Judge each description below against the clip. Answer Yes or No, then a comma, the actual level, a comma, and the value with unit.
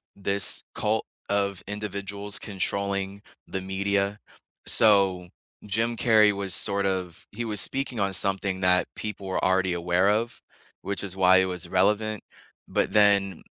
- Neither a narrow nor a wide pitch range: No, narrow, 1.6 semitones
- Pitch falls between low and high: No, low, 100 Hz